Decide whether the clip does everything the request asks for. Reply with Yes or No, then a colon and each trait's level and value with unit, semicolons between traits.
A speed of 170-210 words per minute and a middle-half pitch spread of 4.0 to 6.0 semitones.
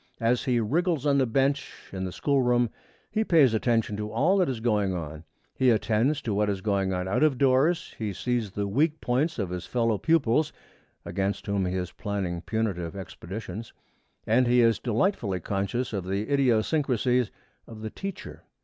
Yes: average, 180 wpm; average, 5.1 semitones